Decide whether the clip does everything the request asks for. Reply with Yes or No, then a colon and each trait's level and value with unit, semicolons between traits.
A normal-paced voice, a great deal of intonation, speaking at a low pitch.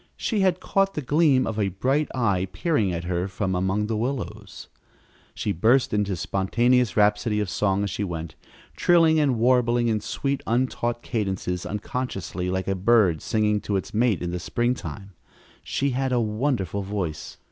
No: average, 170 wpm; average, 4.7 semitones; low, 105 Hz